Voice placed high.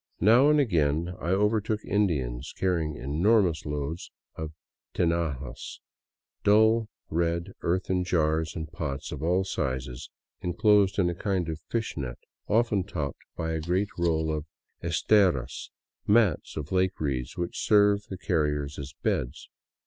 No: very low, 85 Hz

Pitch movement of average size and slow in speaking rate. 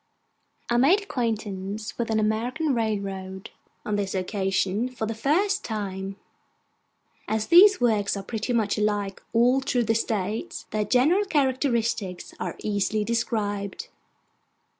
Yes: average, 3.5 semitones; slow, 125 wpm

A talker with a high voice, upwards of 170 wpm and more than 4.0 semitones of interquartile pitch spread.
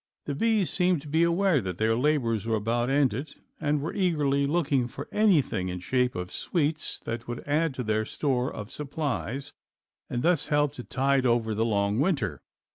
No: low, 135 Hz; average, 185 wpm; average, 4.8 semitones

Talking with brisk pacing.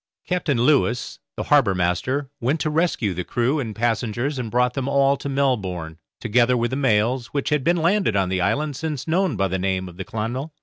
Yes: fast, 210 wpm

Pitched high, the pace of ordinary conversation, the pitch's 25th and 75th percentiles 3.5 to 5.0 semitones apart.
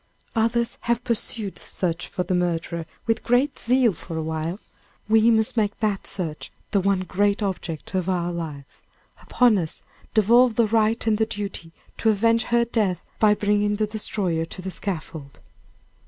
Yes: high, 205 Hz; average, 170 wpm; average, 4.2 semitones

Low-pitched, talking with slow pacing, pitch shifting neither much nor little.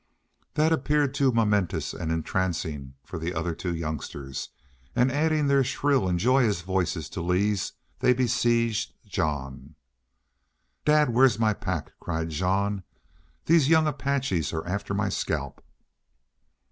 No: low, 100 Hz; slow, 130 wpm; wide, 7.8 semitones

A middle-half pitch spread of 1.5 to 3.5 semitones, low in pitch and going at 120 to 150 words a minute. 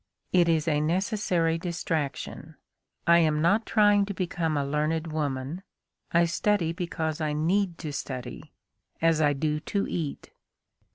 No: average, 2.7 semitones; medium, 165 Hz; average, 140 wpm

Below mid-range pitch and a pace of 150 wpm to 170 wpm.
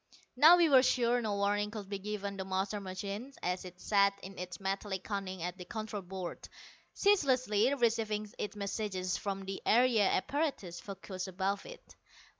No: high, 200 Hz; average, 165 wpm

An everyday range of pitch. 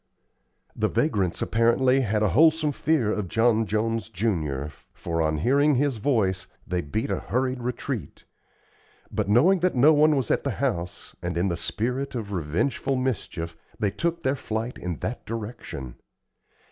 No: wide, 6.0 semitones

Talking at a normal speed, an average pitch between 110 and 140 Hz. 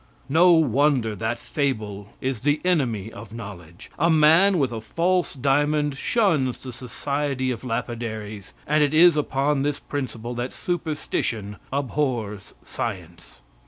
No: slow, 130 wpm; low, 135 Hz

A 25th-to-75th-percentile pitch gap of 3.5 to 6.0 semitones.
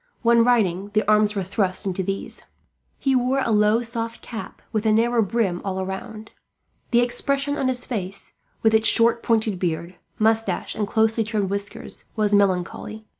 No: average, 2.8 semitones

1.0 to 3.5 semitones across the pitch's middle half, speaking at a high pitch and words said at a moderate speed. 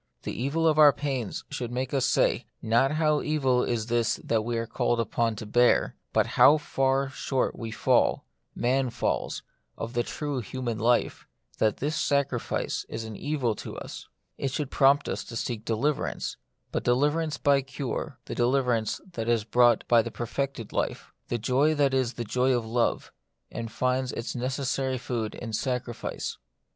No: average, 2.9 semitones; low, 125 Hz; average, 175 wpm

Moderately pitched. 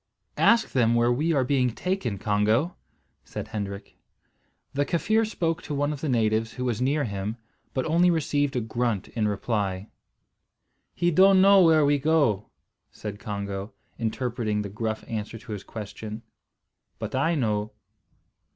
No: low, 120 Hz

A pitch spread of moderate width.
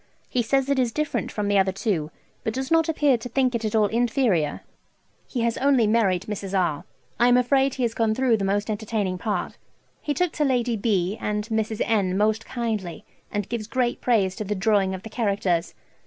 Yes: average, 3.7 semitones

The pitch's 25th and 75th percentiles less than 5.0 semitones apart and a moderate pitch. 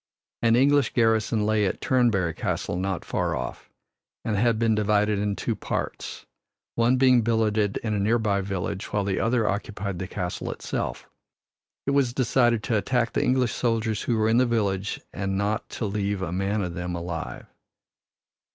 No: average, 3.0 semitones; low, 105 Hz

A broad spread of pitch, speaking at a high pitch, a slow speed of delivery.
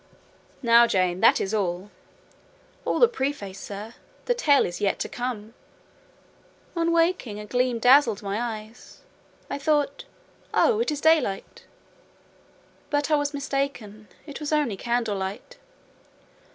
Yes: wide, 5.9 semitones; high, 245 Hz; slow, 125 wpm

